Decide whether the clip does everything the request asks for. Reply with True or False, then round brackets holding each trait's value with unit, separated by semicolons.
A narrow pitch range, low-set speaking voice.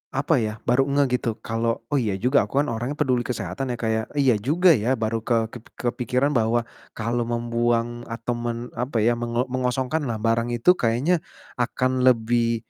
True (1.9 semitones; 120 Hz)